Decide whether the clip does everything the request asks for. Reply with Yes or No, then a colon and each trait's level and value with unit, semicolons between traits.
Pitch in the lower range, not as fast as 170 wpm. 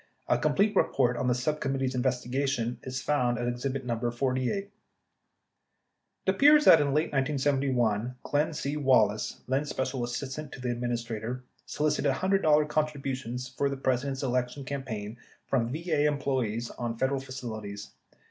Yes: low, 130 Hz; average, 150 wpm